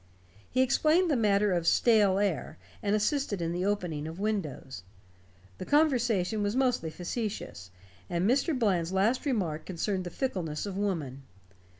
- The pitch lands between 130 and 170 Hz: No, high, 200 Hz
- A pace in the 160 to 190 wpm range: No, average, 150 wpm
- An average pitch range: No, wide, 5.7 semitones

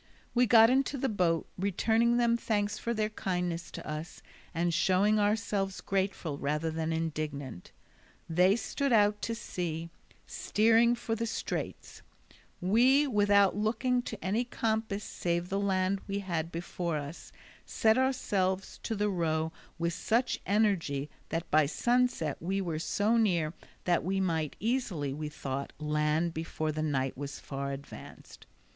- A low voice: No, high, 190 Hz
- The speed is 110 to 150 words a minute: Yes, average, 145 wpm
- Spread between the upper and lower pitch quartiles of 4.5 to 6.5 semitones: Yes, wide, 5.4 semitones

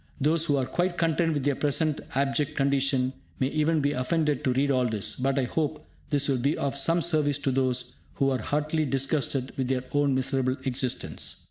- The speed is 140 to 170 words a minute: No, average, 200 wpm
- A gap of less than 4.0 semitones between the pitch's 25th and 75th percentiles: Yes, narrow, 2.5 semitones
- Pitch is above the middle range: No, medium, 140 Hz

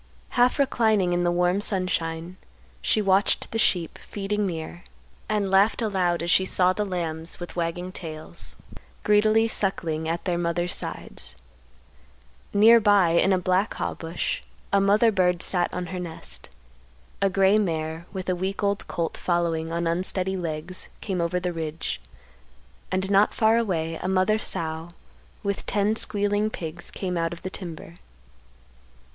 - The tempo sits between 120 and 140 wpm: No, average, 155 wpm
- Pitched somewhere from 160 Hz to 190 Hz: Yes, medium, 185 Hz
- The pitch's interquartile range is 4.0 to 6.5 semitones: No, average, 3.1 semitones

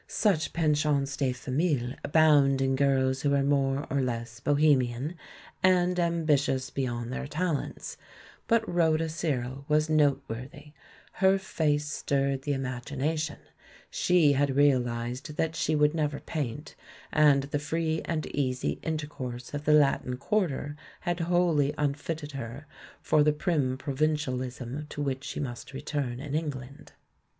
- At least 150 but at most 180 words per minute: No, average, 140 wpm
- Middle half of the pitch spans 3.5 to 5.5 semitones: No, narrow, 2.6 semitones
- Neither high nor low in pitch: Yes, medium, 145 Hz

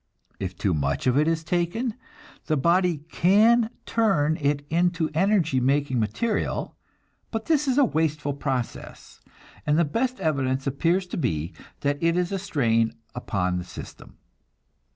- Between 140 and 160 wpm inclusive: Yes, average, 150 wpm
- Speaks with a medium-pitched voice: Yes, medium, 155 Hz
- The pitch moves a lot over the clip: Yes, wide, 5.8 semitones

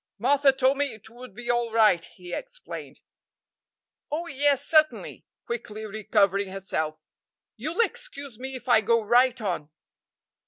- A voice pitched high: Yes, high, 240 Hz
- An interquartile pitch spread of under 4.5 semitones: No, average, 4.9 semitones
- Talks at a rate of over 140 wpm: No, slow, 135 wpm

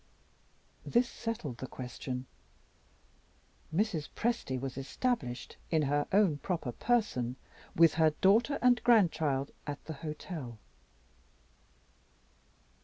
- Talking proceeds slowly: Yes, slow, 100 wpm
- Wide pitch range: Yes, wide, 8.1 semitones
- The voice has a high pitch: No, medium, 155 Hz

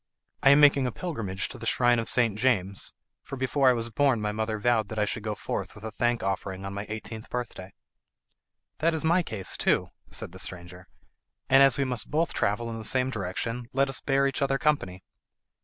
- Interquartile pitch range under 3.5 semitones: No, average, 4.6 semitones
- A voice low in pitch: Yes, low, 115 Hz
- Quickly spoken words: Yes, fast, 215 wpm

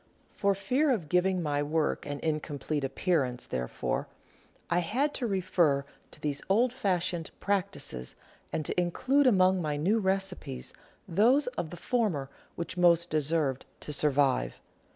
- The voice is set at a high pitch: No, medium, 170 Hz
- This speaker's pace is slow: No, average, 145 wpm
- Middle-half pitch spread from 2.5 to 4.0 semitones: No, average, 5.2 semitones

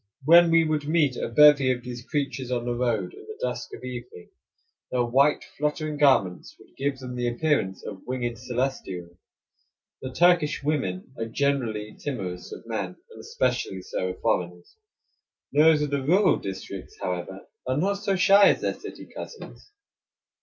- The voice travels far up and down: No, average, 4.8 semitones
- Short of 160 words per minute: No, average, 165 wpm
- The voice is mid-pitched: No, low, 130 Hz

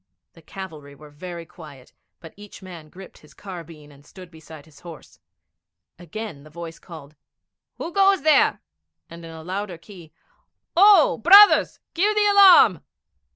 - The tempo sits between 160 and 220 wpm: No, average, 150 wpm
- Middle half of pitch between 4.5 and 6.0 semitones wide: Yes, average, 5.3 semitones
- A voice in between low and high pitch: Yes, medium, 170 Hz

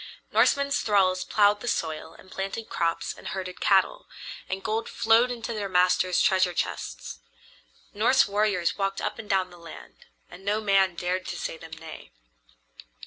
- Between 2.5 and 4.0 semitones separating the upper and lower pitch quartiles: Yes, average, 2.8 semitones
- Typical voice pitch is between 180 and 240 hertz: Yes, high, 190 Hz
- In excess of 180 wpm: No, average, 160 wpm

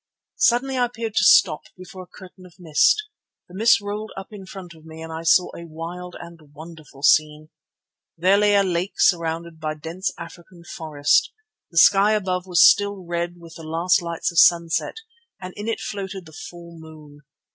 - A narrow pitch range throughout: No, average, 3.0 semitones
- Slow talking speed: No, average, 185 wpm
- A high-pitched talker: No, medium, 175 Hz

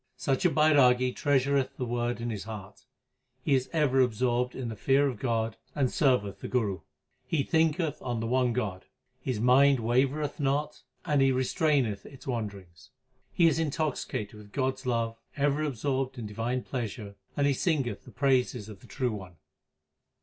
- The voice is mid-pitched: No, low, 130 Hz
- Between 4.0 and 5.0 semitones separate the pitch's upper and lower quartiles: No, average, 3.6 semitones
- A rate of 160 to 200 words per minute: Yes, average, 170 wpm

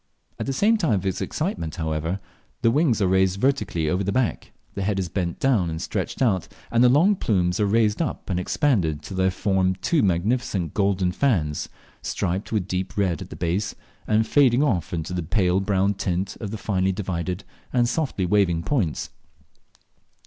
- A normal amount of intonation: Yes, average, 4.3 semitones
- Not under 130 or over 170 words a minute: No, average, 185 wpm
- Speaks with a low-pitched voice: Yes, very low, 95 Hz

